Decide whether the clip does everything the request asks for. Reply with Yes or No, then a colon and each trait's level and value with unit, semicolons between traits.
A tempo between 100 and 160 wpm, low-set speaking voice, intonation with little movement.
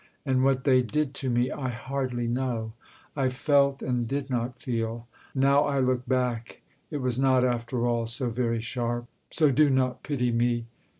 No: average, 175 wpm; low, 125 Hz; narrow, 2.1 semitones